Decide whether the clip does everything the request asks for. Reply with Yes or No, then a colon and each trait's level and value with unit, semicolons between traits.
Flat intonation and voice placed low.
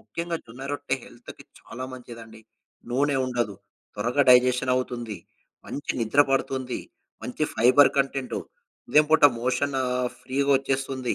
Yes: narrow, 2.1 semitones; low, 130 Hz